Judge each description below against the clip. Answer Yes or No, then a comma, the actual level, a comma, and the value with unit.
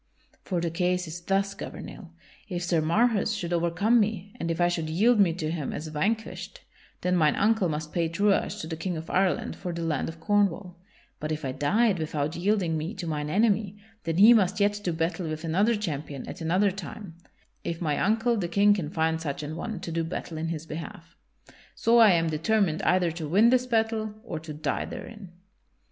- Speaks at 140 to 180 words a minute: No, fast, 205 wpm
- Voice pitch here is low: No, medium, 175 Hz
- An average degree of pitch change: Yes, average, 4.2 semitones